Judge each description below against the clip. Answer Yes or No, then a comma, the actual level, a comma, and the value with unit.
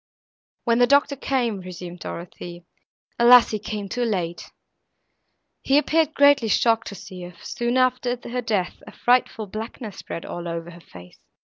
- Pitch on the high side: Yes, high, 220 Hz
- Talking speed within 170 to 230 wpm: No, average, 160 wpm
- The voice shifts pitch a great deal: Yes, wide, 5.8 semitones